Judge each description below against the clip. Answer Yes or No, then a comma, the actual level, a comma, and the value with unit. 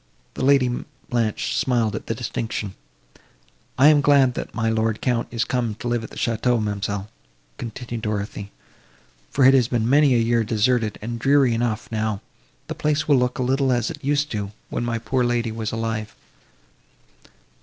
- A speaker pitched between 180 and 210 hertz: No, low, 120 Hz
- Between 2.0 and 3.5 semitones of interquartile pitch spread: Yes, narrow, 2.5 semitones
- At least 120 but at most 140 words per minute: No, average, 185 wpm